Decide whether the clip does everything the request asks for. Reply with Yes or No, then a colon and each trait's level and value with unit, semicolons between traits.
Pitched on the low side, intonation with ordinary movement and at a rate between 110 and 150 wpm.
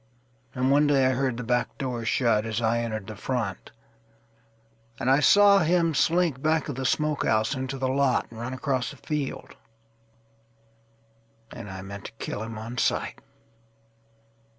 Yes: low, 120 Hz; average, 3.2 semitones; average, 145 wpm